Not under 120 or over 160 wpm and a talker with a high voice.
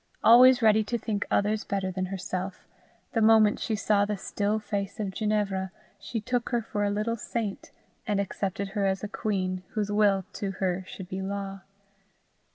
No: average, 175 wpm; high, 205 Hz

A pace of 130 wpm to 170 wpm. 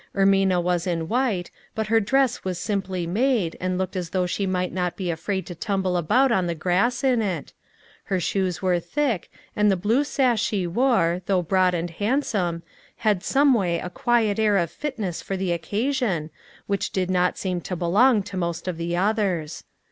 No: average, 190 wpm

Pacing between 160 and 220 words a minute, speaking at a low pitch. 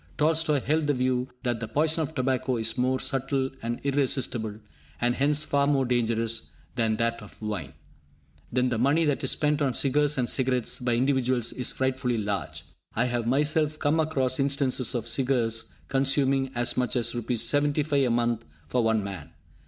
Yes: average, 175 wpm; low, 130 Hz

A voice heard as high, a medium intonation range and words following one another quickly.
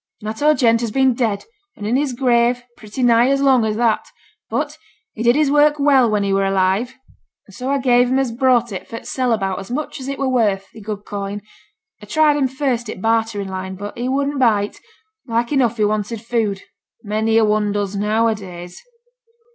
Yes: high, 230 Hz; average, 3.9 semitones; fast, 215 wpm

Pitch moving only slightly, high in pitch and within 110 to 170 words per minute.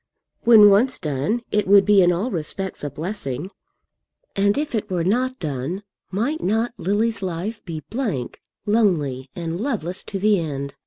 No: average, 5.0 semitones; high, 195 Hz; average, 160 wpm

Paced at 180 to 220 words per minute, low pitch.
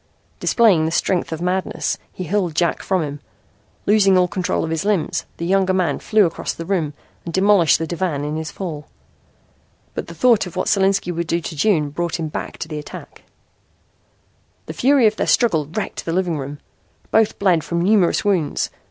No: average, 190 wpm; medium, 175 Hz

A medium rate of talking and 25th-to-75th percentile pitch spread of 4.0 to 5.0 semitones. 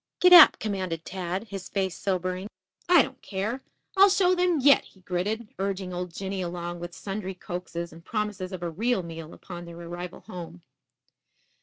No: average, 170 wpm; average, 3.4 semitones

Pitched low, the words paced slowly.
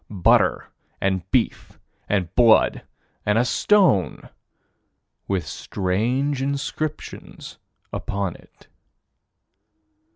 Yes: low, 105 Hz; slow, 75 wpm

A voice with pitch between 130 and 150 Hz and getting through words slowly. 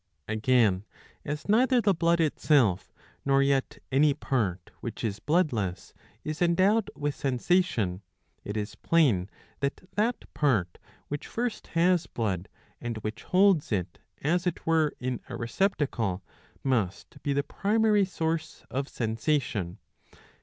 Yes: medium, 140 Hz; slow, 130 wpm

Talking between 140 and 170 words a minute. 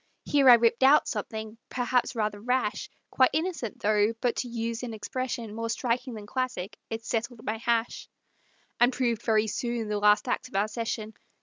No: average, 180 wpm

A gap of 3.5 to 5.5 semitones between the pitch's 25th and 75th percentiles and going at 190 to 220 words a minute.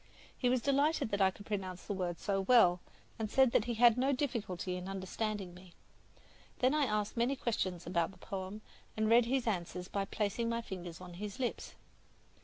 Yes: average, 4.4 semitones; average, 195 wpm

